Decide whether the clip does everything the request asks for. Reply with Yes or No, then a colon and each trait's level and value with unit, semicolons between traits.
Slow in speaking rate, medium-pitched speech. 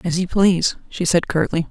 No: fast, 210 wpm; medium, 175 Hz